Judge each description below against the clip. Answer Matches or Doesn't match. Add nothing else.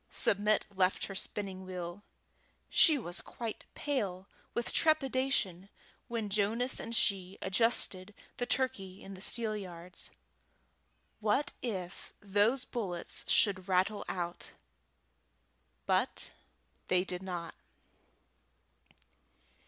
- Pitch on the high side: Matches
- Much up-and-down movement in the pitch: Doesn't match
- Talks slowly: Matches